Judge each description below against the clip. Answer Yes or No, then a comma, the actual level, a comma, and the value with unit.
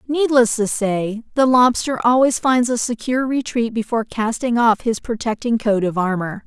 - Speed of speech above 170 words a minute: No, average, 165 wpm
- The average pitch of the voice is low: No, high, 230 Hz